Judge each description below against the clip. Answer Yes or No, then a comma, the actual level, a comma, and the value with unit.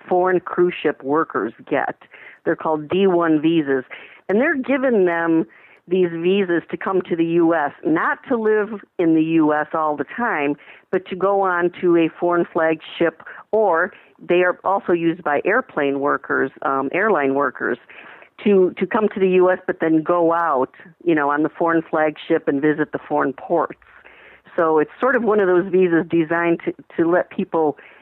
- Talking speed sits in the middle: Yes, average, 175 wpm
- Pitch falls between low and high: Yes, medium, 170 Hz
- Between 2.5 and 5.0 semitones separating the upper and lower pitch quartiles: Yes, average, 2.8 semitones